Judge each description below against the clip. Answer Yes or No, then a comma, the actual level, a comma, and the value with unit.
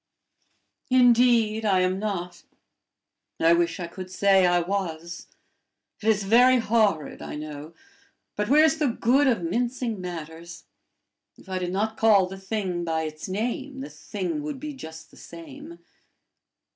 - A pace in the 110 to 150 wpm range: Yes, average, 145 wpm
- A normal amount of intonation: No, wide, 5.9 semitones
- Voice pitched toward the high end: Yes, high, 200 Hz